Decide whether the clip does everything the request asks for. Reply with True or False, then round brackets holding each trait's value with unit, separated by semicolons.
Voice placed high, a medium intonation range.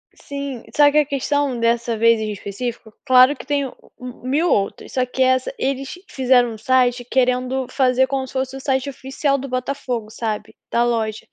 False (255 Hz; 2.2 semitones)